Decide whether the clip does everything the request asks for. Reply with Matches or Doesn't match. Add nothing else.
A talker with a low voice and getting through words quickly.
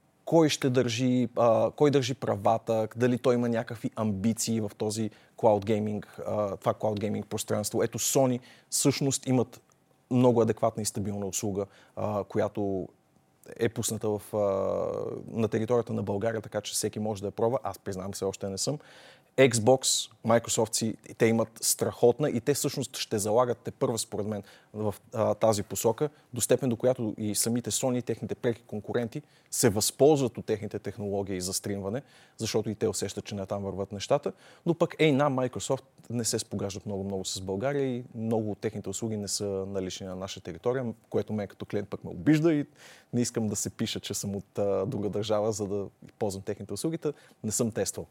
Matches